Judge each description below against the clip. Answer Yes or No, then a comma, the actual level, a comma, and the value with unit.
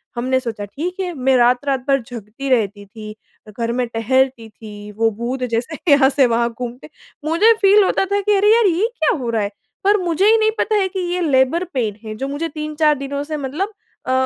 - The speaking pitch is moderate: No, very high, 265 Hz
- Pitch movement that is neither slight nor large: No, wide, 6.1 semitones